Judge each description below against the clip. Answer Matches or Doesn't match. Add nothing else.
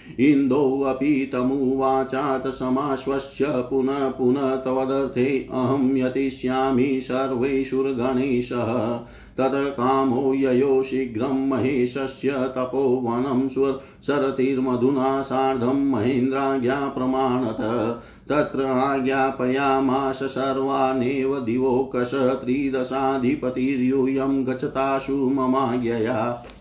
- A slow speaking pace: Matches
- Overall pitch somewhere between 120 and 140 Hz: Matches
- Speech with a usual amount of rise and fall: Doesn't match